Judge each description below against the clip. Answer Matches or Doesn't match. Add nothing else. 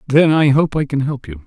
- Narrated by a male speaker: Matches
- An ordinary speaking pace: Doesn't match